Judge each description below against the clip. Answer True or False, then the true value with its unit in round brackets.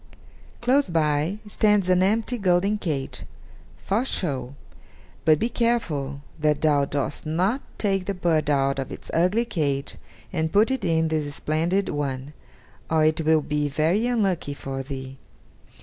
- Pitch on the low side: False (160 Hz)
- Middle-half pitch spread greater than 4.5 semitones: True (5.4 semitones)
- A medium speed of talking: True (150 wpm)